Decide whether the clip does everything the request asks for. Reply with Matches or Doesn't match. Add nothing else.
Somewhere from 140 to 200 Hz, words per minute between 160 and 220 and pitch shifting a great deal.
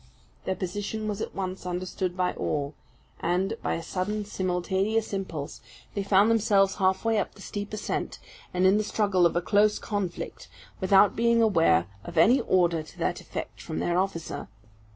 Doesn't match